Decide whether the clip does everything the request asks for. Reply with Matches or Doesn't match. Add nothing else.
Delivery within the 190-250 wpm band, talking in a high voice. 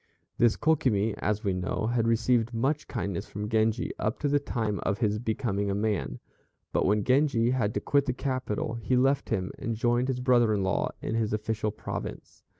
Doesn't match